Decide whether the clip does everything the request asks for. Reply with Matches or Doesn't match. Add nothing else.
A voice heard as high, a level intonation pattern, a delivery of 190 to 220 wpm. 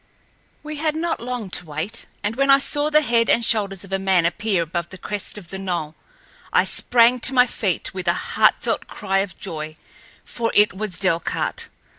Doesn't match